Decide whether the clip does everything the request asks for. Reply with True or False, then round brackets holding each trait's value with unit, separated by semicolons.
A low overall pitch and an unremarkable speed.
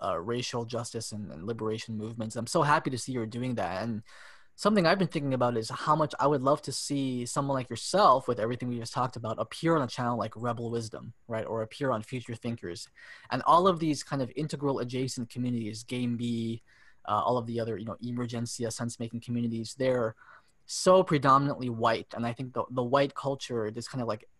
False (120 Hz; 215 wpm)